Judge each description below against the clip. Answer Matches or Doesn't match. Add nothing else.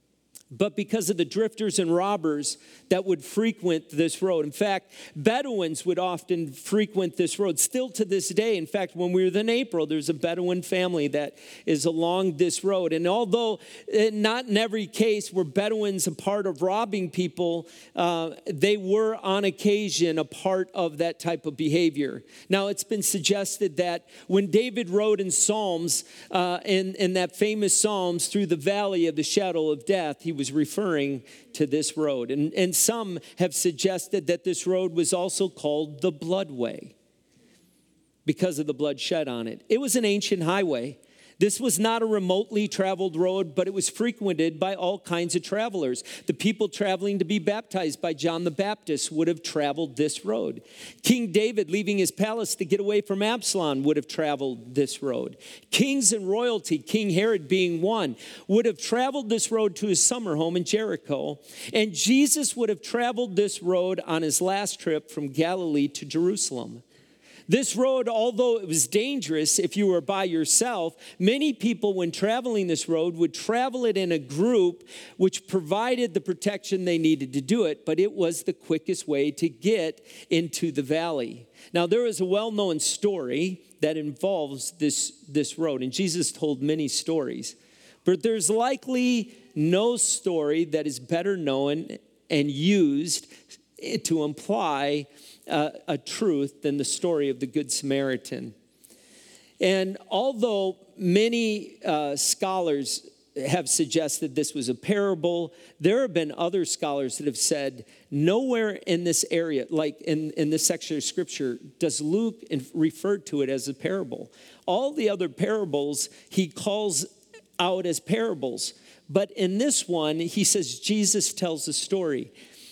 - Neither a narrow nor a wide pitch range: Matches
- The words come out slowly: Doesn't match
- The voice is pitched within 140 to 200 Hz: Matches